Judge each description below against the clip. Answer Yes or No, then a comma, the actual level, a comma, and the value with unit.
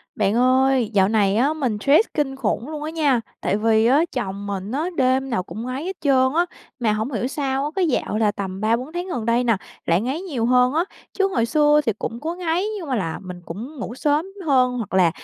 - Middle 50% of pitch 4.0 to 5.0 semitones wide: No, wide, 5.4 semitones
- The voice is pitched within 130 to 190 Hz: No, very high, 255 Hz